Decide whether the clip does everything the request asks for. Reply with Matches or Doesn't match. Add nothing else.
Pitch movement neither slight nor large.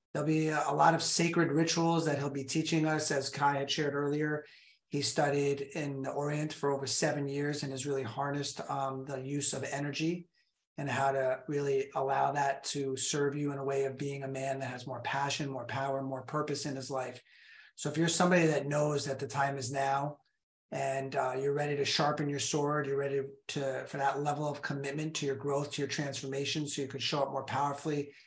Doesn't match